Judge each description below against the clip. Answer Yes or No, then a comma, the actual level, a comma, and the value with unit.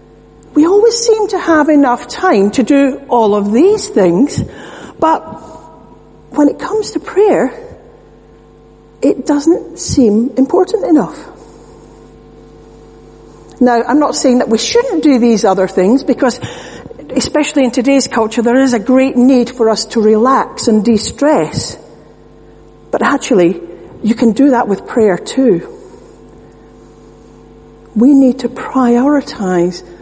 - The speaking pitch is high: Yes, very high, 260 Hz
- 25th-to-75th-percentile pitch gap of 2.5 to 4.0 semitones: No, average, 4.7 semitones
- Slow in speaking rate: Yes, slow, 130 wpm